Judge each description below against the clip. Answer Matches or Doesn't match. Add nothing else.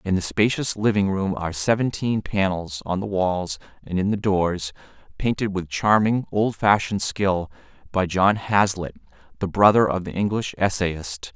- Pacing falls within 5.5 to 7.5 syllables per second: Doesn't match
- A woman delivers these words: Doesn't match